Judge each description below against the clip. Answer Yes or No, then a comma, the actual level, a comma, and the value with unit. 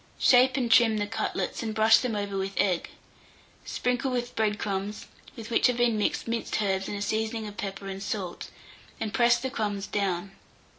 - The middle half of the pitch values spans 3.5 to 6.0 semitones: No, average, 2.9 semitones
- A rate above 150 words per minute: Yes, average, 190 wpm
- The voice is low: No, high, 215 Hz